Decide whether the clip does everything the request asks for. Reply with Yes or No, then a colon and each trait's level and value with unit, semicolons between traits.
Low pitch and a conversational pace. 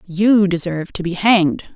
No: medium, 185 Hz; average, 170 wpm